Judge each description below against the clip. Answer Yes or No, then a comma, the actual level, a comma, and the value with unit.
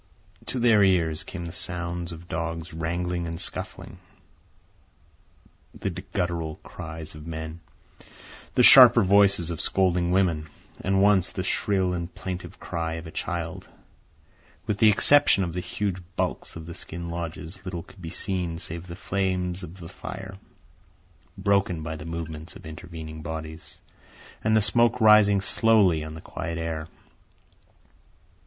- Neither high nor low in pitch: No, very low, 85 Hz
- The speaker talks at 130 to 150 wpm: Yes, average, 145 wpm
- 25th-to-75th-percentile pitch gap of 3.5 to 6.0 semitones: No, average, 2.7 semitones